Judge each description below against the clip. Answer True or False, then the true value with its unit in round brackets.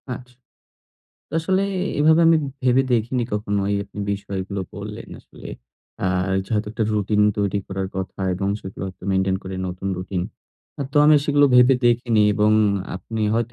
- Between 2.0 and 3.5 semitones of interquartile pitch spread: False (4.4 semitones)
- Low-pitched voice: True (105 Hz)